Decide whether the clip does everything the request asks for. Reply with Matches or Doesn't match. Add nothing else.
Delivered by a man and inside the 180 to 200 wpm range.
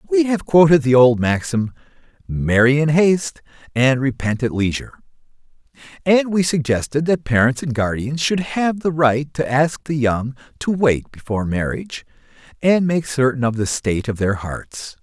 Doesn't match